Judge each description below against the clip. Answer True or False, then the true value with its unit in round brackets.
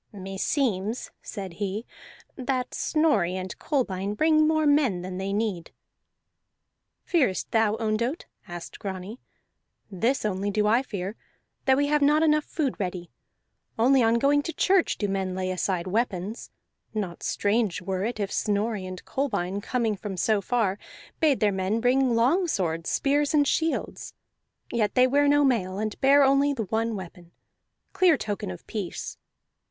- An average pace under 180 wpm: True (150 wpm)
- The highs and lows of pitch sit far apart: True (6.2 semitones)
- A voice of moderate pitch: False (220 Hz)